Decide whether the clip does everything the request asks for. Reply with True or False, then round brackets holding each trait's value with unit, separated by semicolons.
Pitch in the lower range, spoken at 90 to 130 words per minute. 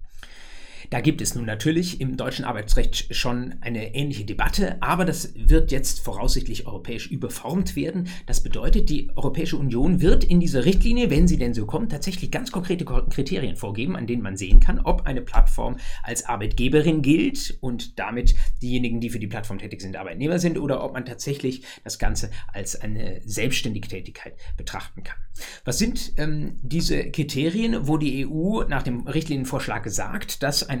False (130 Hz; 170 wpm)